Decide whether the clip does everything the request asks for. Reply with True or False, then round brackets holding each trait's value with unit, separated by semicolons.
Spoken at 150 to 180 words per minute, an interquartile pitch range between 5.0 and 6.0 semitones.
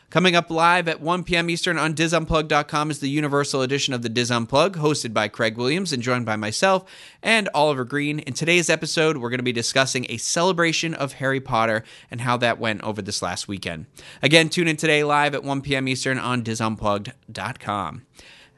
False (190 wpm; 5.4 semitones)